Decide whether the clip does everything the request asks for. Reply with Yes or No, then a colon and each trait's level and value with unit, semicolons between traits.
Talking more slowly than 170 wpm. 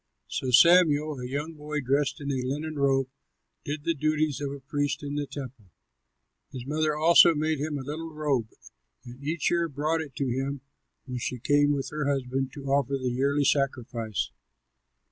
No: average, 185 wpm